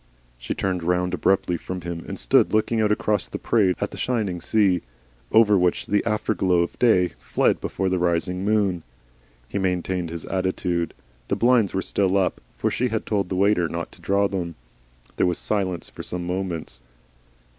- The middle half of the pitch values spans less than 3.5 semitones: Yes, average, 2.7 semitones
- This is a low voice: Yes, very low, 95 Hz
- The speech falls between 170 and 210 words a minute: Yes, average, 180 wpm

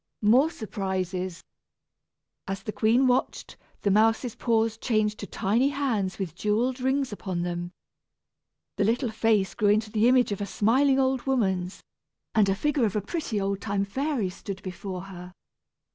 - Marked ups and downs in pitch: No, average, 4.2 semitones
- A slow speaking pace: No, average, 160 wpm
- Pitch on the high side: Yes, high, 215 Hz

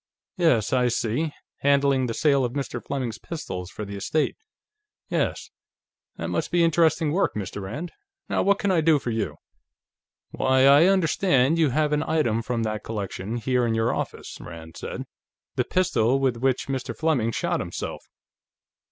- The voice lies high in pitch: No, low, 130 Hz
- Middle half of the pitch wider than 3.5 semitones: Yes, wide, 5.6 semitones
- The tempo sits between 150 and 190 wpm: Yes, average, 165 wpm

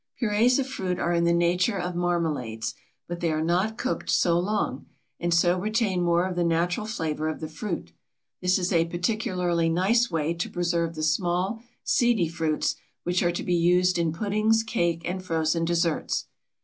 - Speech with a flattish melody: Yes, narrow, 2.1 semitones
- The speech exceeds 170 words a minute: Yes, average, 180 wpm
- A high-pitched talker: No, medium, 175 Hz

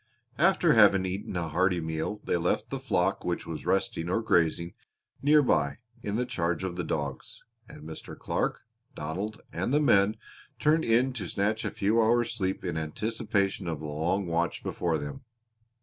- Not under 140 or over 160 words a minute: No, average, 170 wpm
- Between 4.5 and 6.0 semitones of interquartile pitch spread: Yes, average, 4.9 semitones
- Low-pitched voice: Yes, very low, 95 Hz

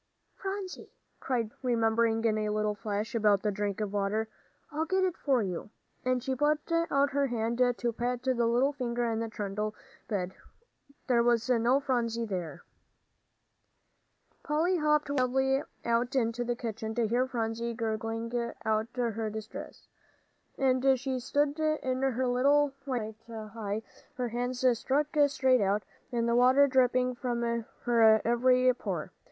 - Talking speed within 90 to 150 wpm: Yes, average, 145 wpm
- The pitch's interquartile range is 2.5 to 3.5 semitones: Yes, average, 2.8 semitones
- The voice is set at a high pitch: Yes, high, 240 Hz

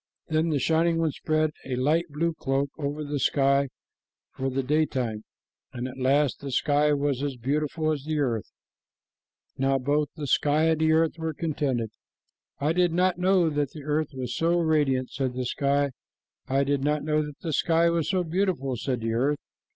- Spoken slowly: No, average, 180 wpm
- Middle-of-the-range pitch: Yes, medium, 145 Hz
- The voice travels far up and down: No, average, 2.8 semitones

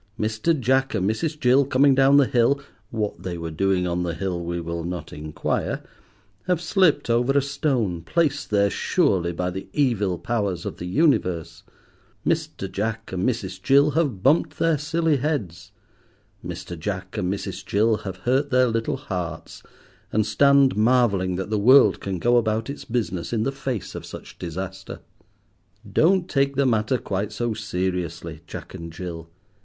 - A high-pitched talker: No, low, 110 Hz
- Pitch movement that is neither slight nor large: No, wide, 6.9 semitones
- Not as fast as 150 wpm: No, average, 160 wpm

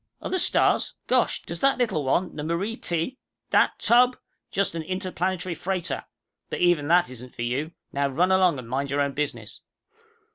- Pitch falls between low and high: Yes, medium, 170 Hz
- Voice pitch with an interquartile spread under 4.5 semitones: No, average, 4.9 semitones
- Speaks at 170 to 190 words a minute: Yes, average, 180 wpm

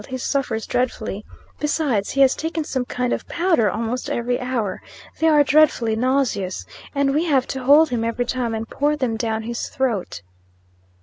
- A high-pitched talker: Yes, very high, 250 Hz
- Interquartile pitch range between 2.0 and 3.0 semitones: No, average, 3.8 semitones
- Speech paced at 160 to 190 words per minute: Yes, average, 175 wpm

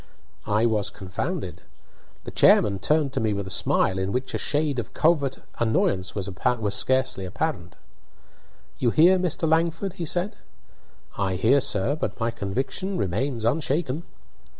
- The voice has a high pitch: No, low, 130 Hz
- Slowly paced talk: No, average, 145 wpm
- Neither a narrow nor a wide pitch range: No, wide, 7.7 semitones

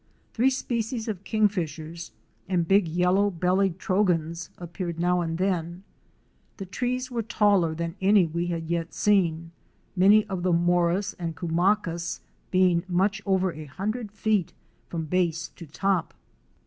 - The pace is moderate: Yes, average, 145 wpm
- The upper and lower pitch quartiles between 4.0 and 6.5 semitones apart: No, average, 3.2 semitones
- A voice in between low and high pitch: Yes, medium, 180 Hz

